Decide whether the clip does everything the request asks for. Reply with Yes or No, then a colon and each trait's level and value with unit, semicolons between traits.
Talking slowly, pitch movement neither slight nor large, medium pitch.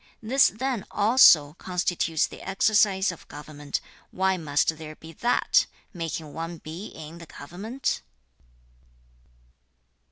Yes: slow, 115 wpm; average, 4.7 semitones; medium, 175 Hz